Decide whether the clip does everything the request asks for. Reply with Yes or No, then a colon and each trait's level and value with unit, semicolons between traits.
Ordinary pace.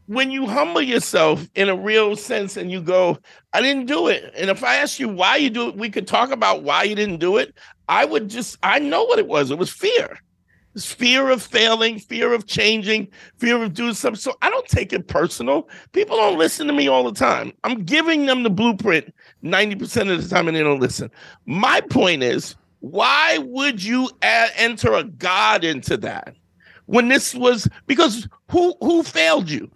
No: fast, 210 wpm